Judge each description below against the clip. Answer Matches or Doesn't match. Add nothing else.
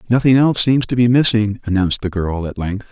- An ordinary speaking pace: Doesn't match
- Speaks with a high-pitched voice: Doesn't match